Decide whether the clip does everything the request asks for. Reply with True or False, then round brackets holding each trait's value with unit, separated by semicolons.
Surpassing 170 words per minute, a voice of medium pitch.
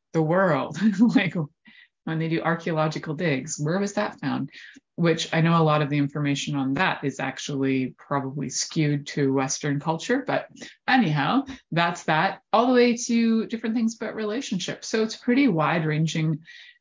False (165 wpm; 165 Hz)